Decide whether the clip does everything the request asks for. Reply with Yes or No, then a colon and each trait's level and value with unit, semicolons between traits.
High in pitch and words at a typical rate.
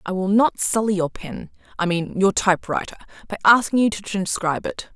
Yes: high, 200 Hz; average, 170 wpm